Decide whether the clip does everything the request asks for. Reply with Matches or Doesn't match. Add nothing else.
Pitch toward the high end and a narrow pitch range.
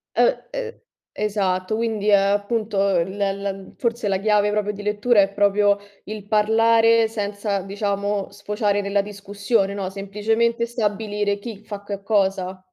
Matches